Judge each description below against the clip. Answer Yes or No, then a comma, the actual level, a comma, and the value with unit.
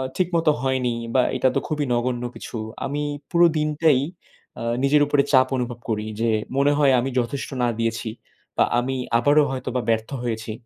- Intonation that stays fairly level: No, average, 3.5 semitones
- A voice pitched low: Yes, low, 130 Hz